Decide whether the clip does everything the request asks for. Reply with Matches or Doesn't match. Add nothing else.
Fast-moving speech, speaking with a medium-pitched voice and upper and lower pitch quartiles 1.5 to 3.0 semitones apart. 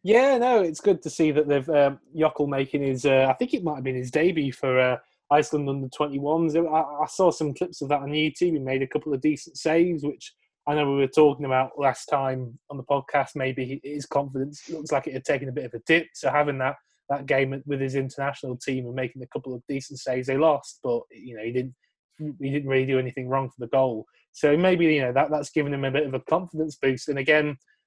Matches